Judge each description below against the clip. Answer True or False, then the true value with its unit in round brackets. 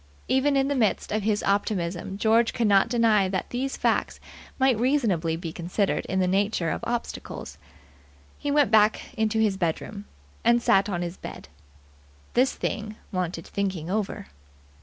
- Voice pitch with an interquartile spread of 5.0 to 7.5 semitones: False (4.0 semitones)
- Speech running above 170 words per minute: False (160 wpm)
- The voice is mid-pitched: False (210 Hz)